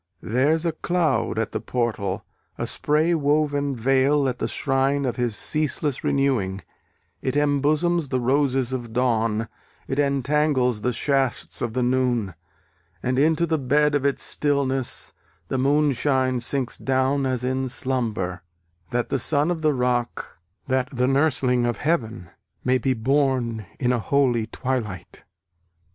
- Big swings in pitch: No, average, 2.7 semitones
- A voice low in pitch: Yes, low, 130 Hz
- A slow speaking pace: No, average, 145 wpm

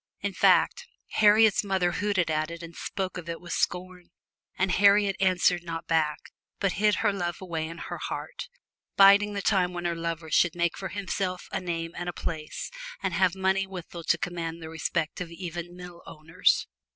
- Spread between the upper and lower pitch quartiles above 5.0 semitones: No, narrow, 2.4 semitones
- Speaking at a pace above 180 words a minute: Yes, average, 190 wpm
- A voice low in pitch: No, medium, 180 Hz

